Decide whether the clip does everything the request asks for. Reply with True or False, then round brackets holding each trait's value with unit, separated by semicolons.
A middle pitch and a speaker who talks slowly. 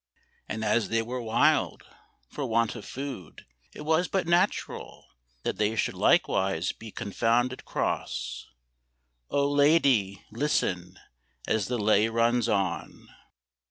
False (115 Hz; 125 wpm)